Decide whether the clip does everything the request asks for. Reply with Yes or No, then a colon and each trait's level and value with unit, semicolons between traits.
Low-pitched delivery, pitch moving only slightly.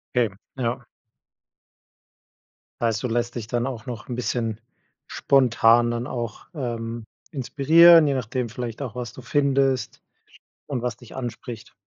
Yes: low, 120 Hz; narrow, 2.1 semitones